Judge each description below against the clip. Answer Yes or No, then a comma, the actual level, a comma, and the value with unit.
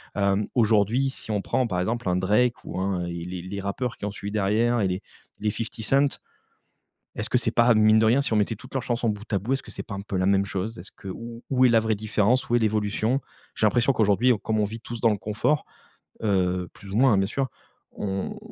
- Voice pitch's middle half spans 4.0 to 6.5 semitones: No, average, 3.1 semitones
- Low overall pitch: Yes, low, 110 Hz